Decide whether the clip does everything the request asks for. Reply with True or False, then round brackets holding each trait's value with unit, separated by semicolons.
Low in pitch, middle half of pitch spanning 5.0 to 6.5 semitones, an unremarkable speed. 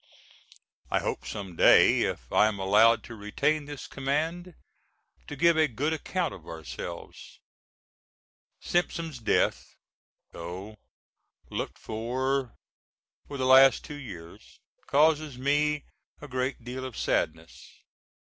False (130 Hz; 5.6 semitones; 120 wpm)